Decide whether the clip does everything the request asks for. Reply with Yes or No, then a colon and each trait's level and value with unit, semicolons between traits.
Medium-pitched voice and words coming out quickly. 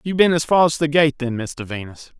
Yes: medium, 145 Hz; fast, 275 wpm